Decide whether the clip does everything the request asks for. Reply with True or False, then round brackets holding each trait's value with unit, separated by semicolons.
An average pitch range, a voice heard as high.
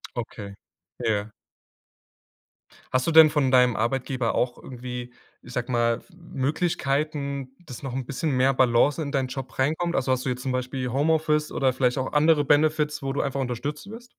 False (3.1 semitones; 135 Hz)